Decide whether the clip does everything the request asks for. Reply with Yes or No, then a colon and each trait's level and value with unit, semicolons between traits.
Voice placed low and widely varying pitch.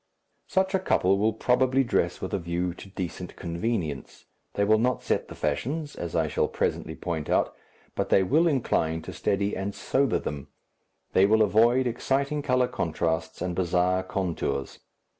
Yes: low, 100 Hz; wide, 6.5 semitones